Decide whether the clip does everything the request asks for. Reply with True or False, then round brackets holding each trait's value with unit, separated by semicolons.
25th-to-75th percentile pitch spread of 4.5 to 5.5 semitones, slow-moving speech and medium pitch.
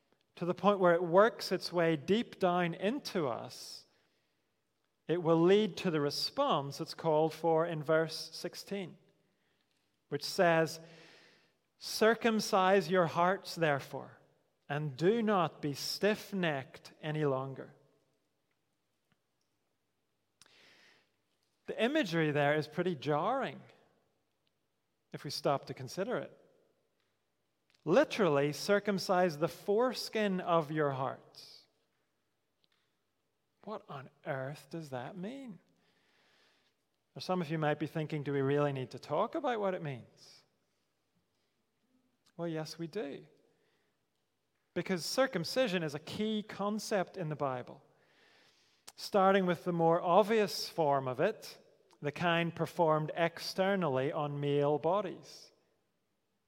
True (4.9 semitones; 115 wpm; 170 Hz)